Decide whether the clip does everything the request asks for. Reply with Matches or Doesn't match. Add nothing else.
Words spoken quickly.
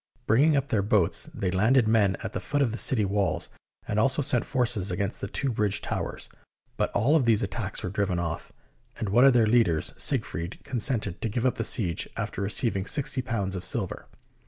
Matches